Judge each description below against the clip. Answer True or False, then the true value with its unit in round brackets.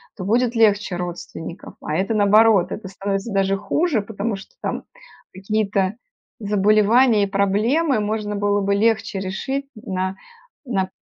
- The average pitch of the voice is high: True (205 Hz)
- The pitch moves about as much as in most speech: False (2.2 semitones)